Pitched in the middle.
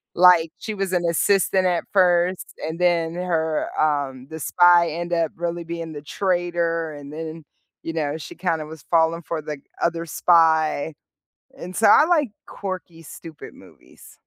Yes: medium, 170 Hz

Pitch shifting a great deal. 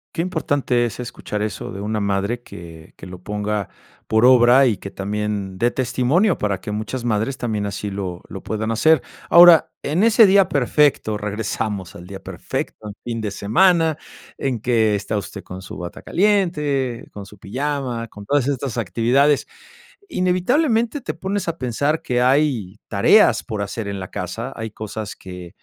Yes: wide, 5.9 semitones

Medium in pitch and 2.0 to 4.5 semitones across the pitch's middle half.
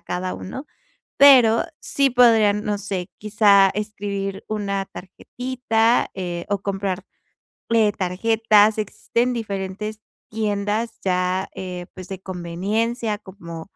No: high, 205 Hz; average, 2.9 semitones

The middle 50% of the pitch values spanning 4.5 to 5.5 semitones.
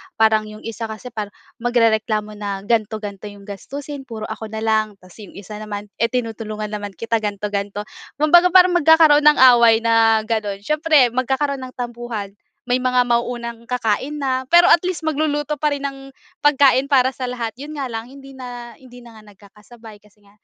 No: average, 4.1 semitones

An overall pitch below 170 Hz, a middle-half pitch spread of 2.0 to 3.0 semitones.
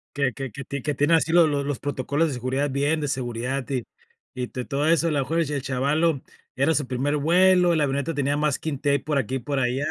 Yes: medium, 140 Hz; narrow, 2.5 semitones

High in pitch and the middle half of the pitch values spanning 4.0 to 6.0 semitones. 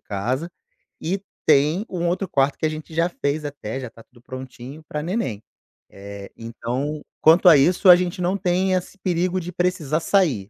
No: medium, 155 Hz; wide, 5.5 semitones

